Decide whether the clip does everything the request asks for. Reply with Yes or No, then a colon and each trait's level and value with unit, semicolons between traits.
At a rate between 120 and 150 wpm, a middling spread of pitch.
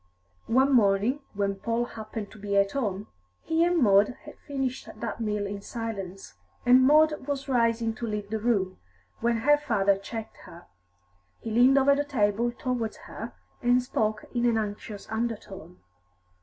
No: average, 160 wpm; average, 3.7 semitones